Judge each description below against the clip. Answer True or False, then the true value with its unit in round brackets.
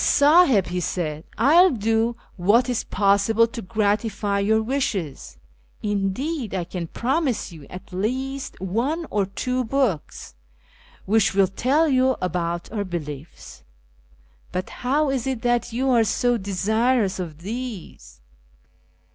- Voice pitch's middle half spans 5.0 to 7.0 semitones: True (5.4 semitones)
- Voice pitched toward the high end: True (220 Hz)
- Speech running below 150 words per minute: True (140 wpm)